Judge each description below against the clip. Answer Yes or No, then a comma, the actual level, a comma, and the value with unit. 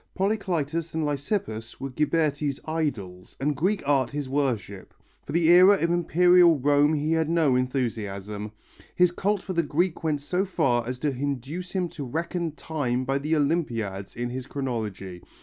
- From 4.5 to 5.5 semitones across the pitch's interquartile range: Yes, average, 5.0 semitones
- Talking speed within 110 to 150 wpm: No, average, 165 wpm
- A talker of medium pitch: Yes, medium, 145 Hz